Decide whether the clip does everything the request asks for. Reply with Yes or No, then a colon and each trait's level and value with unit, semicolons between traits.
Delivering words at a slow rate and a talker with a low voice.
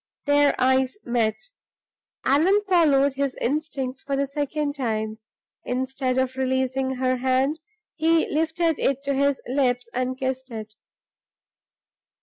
No: slow, 125 wpm; very high, 265 Hz